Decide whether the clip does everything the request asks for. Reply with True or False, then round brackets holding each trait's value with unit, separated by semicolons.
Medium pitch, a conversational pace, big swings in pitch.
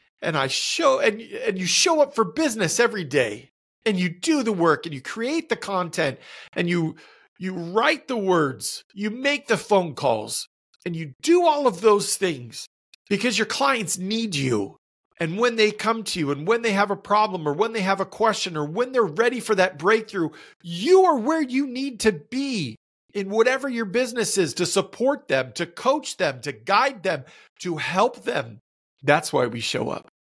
False (215 Hz; 195 wpm; 5.7 semitones)